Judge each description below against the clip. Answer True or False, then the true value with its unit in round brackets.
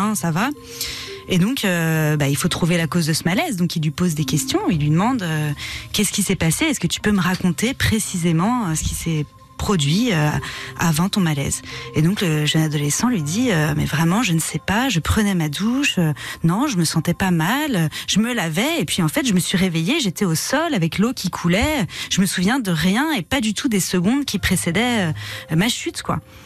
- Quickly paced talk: True (230 wpm)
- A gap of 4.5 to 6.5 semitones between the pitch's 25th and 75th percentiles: True (4.9 semitones)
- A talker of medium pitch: True (180 Hz)